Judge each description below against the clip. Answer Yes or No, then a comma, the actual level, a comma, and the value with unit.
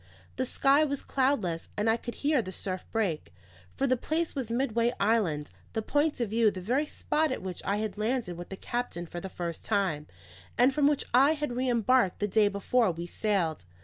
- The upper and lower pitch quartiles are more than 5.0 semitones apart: Yes, wide, 5.6 semitones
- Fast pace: Yes, fast, 210 wpm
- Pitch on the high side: Yes, high, 225 Hz